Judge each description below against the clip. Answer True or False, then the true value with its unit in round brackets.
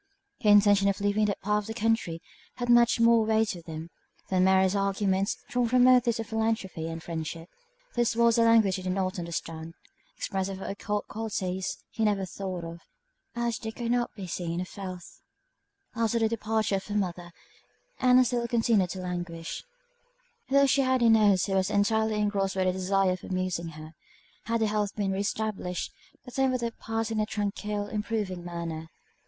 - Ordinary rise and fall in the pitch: True (3.4 semitones)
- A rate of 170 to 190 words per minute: True (185 wpm)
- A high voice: True (205 Hz)